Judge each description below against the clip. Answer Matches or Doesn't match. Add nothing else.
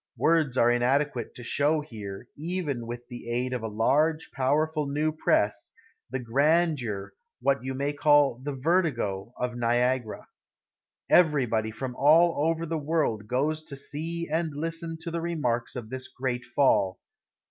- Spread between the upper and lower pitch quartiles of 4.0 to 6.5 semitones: Matches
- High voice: Doesn't match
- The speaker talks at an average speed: Matches